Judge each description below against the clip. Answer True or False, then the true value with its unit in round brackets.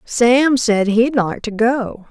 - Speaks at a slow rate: False (170 wpm)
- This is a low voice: False (235 Hz)